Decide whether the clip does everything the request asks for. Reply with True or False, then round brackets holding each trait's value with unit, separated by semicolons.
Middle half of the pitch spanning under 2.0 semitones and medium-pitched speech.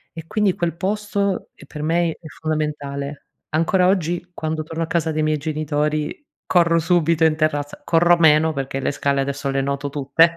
False (2.6 semitones; 155 Hz)